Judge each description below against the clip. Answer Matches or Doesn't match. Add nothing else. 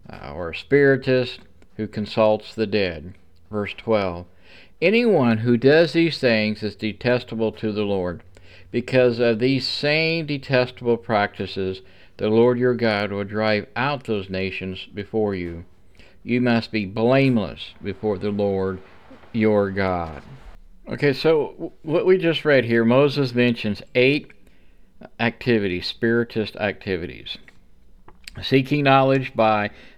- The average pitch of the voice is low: Matches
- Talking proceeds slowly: Matches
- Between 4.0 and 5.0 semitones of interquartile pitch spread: Matches